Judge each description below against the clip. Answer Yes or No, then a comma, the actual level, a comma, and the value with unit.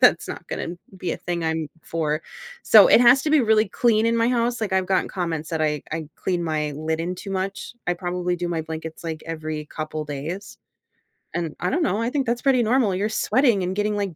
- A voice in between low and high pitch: Yes, medium, 180 Hz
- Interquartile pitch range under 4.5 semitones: No, wide, 5.5 semitones